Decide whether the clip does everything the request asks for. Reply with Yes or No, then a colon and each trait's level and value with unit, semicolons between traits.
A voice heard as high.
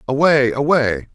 No: low, 135 Hz